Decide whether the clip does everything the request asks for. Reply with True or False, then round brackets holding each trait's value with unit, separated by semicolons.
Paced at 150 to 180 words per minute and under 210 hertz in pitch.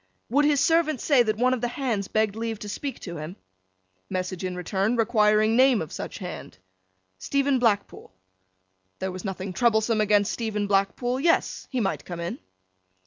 False (170 wpm; 220 Hz)